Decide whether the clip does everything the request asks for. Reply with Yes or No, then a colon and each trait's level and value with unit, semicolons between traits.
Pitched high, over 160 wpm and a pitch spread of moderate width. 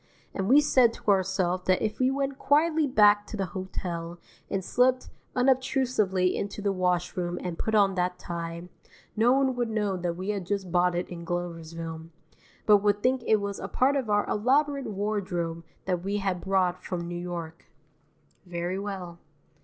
Yes: high, 195 Hz; average, 175 wpm; average, 3.8 semitones